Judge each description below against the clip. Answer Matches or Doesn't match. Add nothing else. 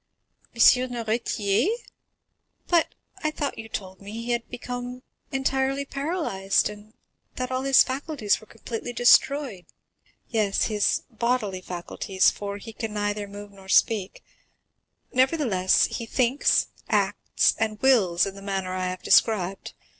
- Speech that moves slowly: Matches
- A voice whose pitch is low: Doesn't match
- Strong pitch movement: Doesn't match